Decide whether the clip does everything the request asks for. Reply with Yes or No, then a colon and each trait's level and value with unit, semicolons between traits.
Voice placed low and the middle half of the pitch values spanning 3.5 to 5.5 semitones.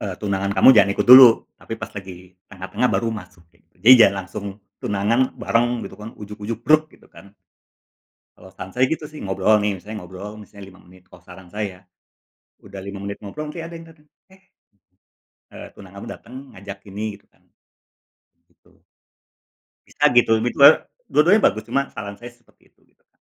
Yes: low, 105 Hz; average, 3.9 semitones